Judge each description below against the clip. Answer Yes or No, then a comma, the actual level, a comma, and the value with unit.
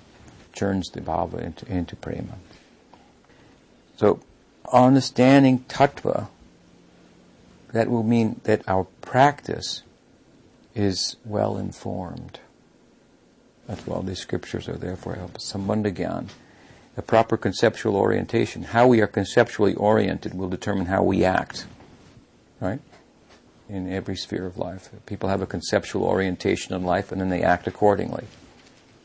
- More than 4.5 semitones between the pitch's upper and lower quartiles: No, average, 3.5 semitones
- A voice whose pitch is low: Yes, low, 100 Hz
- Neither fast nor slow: No, slow, 120 wpm